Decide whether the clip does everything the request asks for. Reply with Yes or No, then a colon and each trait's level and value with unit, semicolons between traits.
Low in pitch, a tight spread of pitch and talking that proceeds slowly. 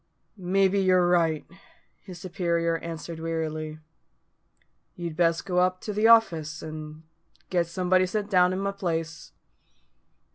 No: medium, 175 Hz; narrow, 2.3 semitones; slow, 130 wpm